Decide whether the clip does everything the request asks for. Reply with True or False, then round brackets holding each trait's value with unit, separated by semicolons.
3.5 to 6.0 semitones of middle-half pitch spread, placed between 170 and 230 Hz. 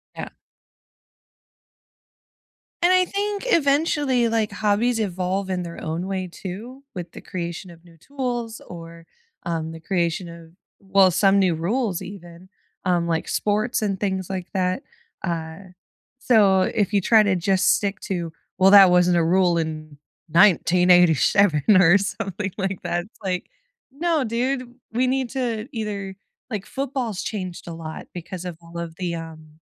True (4.3 semitones; 190 Hz)